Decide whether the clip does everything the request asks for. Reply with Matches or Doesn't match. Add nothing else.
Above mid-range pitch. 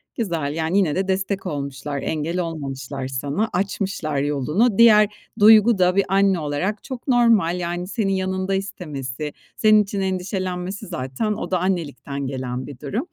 Doesn't match